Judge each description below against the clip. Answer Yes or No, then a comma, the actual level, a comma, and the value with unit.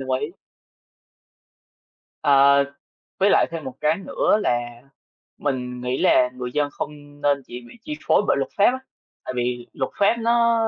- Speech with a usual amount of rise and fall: Yes, average, 4.7 semitones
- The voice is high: No, medium, 140 Hz